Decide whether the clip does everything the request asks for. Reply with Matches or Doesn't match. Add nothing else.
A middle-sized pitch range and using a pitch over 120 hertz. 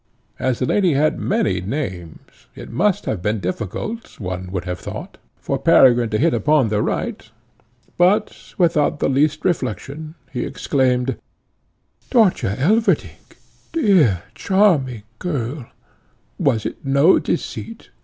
Doesn't match